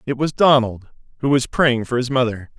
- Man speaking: Yes, male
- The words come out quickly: Yes, fast, 210 wpm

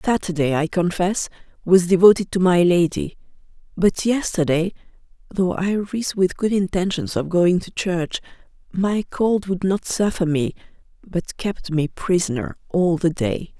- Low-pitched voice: No, medium, 180 Hz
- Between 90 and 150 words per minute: Yes, average, 145 wpm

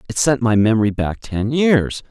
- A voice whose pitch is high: No, low, 120 Hz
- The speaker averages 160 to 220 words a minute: Yes, average, 200 wpm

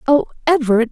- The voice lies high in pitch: Yes, very high, 260 Hz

